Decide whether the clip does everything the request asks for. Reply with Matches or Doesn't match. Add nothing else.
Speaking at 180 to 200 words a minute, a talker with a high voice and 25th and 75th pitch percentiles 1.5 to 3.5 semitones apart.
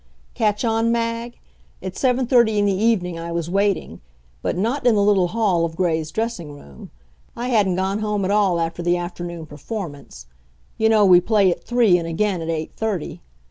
Doesn't match